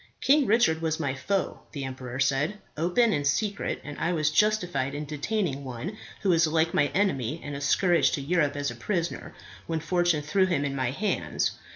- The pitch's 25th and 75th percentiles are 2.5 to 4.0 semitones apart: No, average, 4.4 semitones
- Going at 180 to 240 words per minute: Yes, average, 195 wpm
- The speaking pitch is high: No, medium, 155 Hz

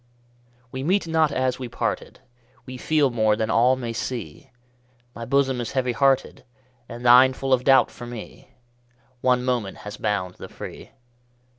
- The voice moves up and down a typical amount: No, narrow, 2.2 semitones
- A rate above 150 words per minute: Yes, average, 160 wpm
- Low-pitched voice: Yes, low, 125 Hz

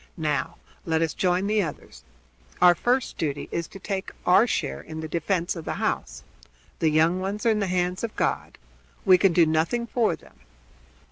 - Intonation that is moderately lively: Yes, average, 3.8 semitones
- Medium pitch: Yes, medium, 180 Hz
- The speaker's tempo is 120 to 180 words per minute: No, average, 190 wpm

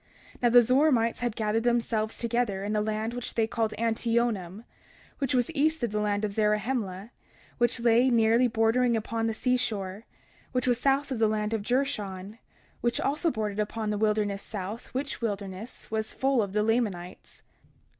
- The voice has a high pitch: Yes, high, 225 Hz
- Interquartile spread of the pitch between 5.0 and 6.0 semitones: No, narrow, 2.4 semitones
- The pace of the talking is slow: No, average, 175 wpm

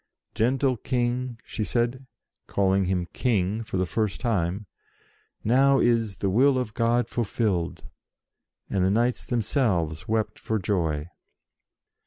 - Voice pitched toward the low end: Yes, low, 110 Hz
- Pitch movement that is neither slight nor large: Yes, average, 4.3 semitones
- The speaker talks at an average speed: No, slow, 125 wpm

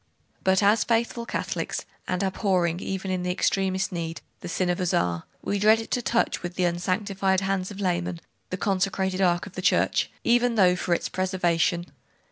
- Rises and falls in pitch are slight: Yes, narrow, 1.9 semitones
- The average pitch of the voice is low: No, medium, 185 Hz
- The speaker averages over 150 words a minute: Yes, average, 175 wpm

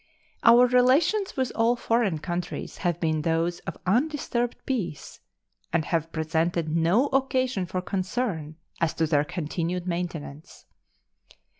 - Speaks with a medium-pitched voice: Yes, medium, 180 Hz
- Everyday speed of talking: No, slow, 125 wpm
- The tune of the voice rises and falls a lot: Yes, wide, 6.9 semitones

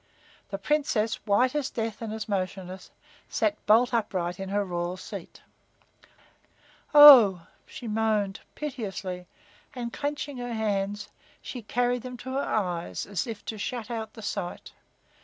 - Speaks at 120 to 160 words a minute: Yes, average, 140 wpm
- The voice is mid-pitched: No, high, 220 Hz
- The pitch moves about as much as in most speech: Yes, average, 4.0 semitones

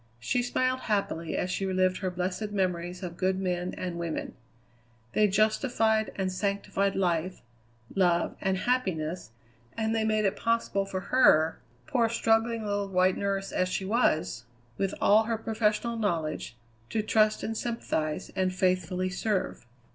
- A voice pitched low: No, high, 195 Hz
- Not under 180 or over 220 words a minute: No, average, 145 wpm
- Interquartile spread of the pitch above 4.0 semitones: No, average, 3.1 semitones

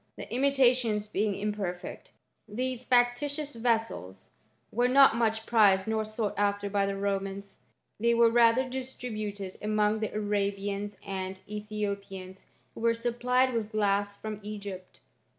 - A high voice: Yes, high, 215 Hz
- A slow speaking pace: Yes, slow, 130 wpm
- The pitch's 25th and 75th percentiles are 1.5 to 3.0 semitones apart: Yes, average, 2.7 semitones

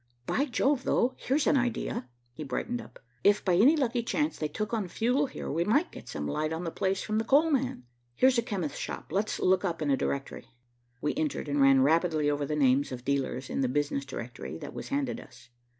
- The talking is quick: Yes, fast, 220 wpm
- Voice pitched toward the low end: No, medium, 175 Hz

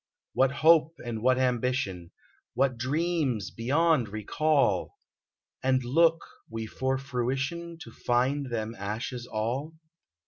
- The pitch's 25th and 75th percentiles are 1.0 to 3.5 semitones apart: No, average, 4.0 semitones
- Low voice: Yes, low, 130 Hz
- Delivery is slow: Yes, slow, 110 wpm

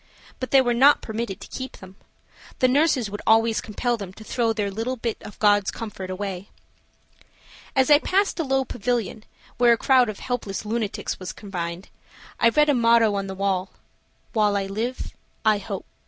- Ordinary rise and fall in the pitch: Yes, average, 3.7 semitones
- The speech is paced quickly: No, average, 185 wpm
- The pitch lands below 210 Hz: No, high, 220 Hz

